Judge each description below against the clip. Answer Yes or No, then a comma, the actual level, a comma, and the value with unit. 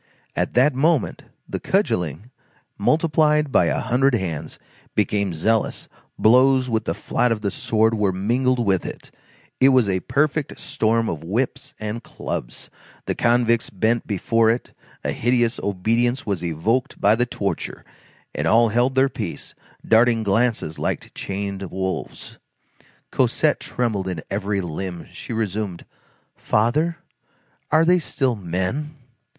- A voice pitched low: Yes, low, 115 Hz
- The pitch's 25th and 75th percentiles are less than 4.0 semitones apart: No, average, 4.4 semitones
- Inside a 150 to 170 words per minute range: No, slow, 135 wpm